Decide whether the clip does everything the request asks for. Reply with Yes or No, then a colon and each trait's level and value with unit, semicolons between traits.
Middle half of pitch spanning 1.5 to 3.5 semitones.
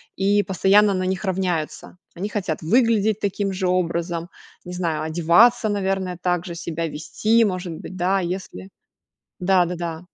Yes: narrow, 2.5 semitones